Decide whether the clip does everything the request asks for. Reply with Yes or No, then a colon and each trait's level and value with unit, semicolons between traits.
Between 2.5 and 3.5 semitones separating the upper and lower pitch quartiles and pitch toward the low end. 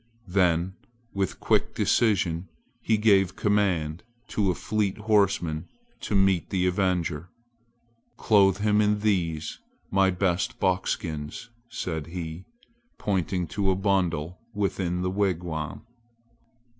Yes: average, 2.9 semitones; very low, 95 Hz